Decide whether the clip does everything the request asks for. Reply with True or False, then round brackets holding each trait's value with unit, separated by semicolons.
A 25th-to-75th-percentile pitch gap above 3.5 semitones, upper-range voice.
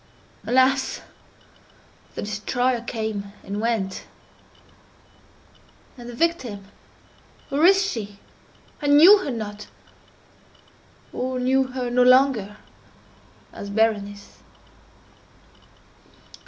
True (4.2 semitones; 240 Hz)